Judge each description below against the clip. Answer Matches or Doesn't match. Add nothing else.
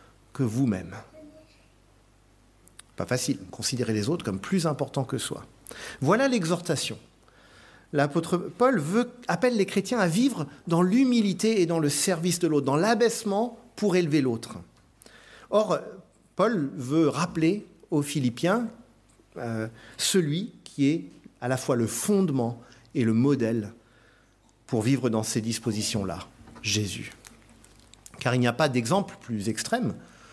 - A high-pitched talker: Doesn't match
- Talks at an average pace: Doesn't match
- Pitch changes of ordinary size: Doesn't match